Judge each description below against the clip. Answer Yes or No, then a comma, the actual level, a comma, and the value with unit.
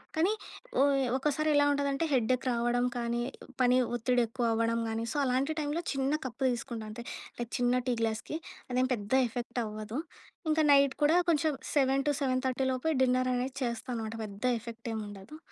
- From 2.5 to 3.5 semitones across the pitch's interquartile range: Yes, average, 2.9 semitones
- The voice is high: Yes, very high, 250 Hz